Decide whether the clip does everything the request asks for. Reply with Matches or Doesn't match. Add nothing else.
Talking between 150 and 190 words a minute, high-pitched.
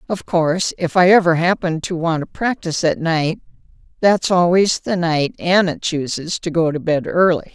Doesn't match